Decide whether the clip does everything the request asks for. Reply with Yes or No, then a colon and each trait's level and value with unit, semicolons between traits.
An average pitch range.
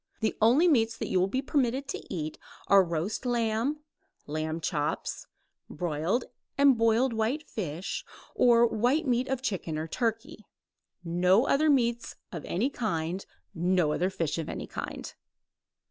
No: wide, 6.4 semitones